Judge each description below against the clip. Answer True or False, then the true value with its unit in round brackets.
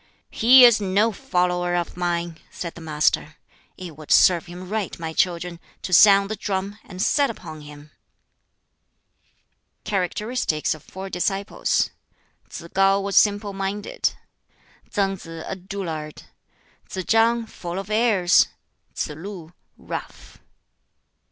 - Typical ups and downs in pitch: True (3.1 semitones)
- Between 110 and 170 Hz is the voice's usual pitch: False (185 Hz)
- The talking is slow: True (125 wpm)